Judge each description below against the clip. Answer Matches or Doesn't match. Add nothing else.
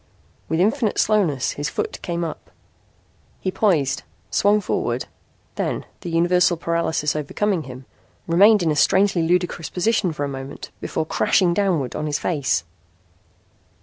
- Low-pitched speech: Doesn't match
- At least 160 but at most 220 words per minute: Doesn't match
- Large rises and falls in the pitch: Doesn't match